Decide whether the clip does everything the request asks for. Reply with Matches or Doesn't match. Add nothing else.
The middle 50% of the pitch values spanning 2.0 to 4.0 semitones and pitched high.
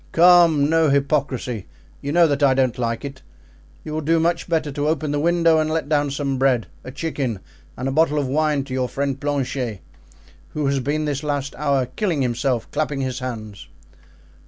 Doesn't match